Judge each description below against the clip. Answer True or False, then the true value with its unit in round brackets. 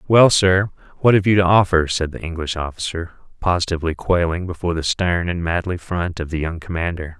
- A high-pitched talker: False (85 Hz)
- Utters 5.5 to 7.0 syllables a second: True (5.7 syllables/s)